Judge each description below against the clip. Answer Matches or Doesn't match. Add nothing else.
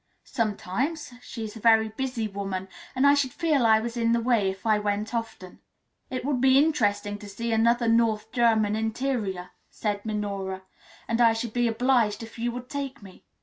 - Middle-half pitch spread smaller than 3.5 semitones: Matches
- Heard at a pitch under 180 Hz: Doesn't match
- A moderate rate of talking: Matches